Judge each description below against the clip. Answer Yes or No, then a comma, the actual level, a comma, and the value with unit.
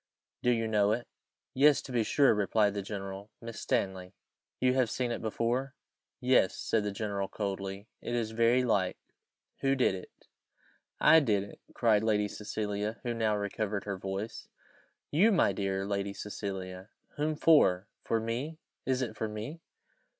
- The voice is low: Yes, low, 110 Hz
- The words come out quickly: No, average, 160 wpm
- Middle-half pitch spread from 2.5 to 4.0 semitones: Yes, average, 3.5 semitones